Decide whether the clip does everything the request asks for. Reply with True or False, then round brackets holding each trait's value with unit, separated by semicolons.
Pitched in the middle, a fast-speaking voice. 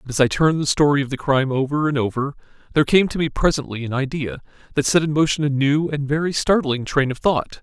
True (145 Hz; 245 wpm)